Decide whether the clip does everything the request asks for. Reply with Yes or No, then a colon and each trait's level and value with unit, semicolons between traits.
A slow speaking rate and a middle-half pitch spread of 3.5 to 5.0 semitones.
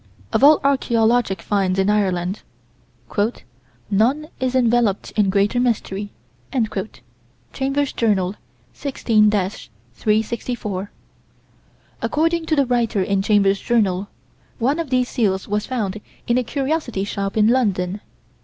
Yes: slow, 115 wpm; average, 4.4 semitones